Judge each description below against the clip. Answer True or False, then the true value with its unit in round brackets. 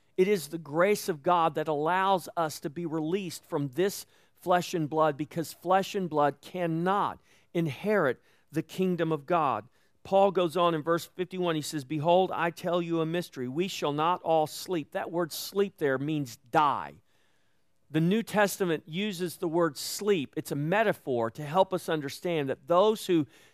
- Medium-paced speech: True (175 wpm)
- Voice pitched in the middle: True (170 Hz)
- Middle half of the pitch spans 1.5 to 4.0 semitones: True (3.0 semitones)